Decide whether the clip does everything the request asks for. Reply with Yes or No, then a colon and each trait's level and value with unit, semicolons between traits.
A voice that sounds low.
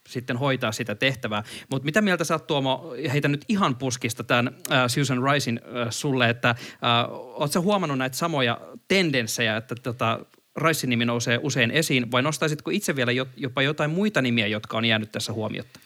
Yes: low, 130 Hz